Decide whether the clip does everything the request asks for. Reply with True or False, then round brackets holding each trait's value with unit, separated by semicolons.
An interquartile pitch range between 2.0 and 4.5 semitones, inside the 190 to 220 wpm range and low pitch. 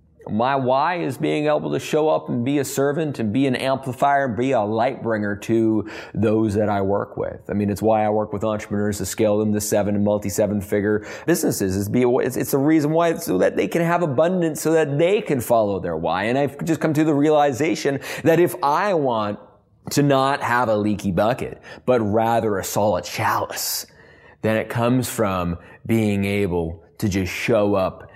False (5.4 semitones; 200 wpm; 110 Hz)